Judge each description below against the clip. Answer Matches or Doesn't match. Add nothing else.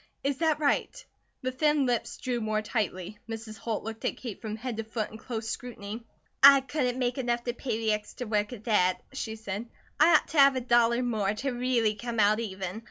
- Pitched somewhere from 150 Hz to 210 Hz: Doesn't match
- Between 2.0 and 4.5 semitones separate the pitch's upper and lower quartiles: Matches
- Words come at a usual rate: Doesn't match